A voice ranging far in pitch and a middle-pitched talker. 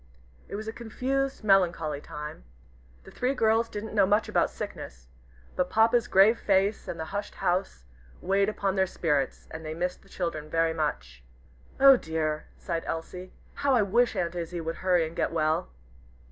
No: average, 5.0 semitones; medium, 180 Hz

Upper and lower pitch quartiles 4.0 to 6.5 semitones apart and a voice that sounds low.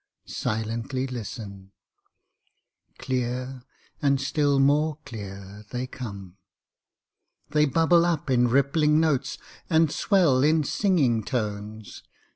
Yes: average, 5.3 semitones; low, 130 Hz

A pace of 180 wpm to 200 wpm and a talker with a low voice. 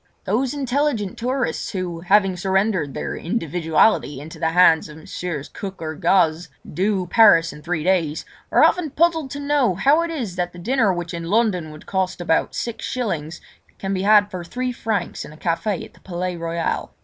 No: average, 185 wpm; medium, 185 Hz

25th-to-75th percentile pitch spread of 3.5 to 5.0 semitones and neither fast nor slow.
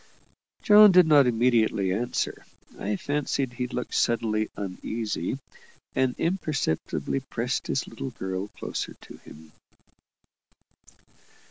No: average, 4.4 semitones; slow, 105 wpm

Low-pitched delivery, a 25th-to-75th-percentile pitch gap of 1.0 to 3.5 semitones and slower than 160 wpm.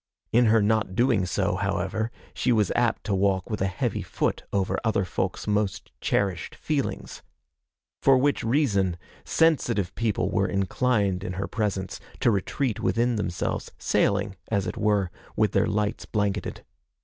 Yes: low, 105 Hz; average, 3.1 semitones; average, 150 wpm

